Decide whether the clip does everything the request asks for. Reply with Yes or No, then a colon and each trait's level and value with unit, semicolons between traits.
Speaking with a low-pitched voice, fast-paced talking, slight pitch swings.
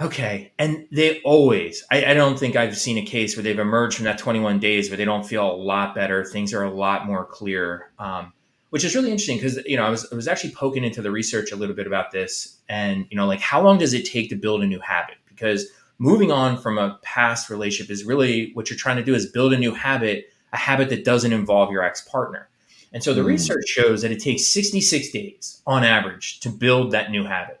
No: low, 110 Hz; fast, 245 wpm; average, 4.5 semitones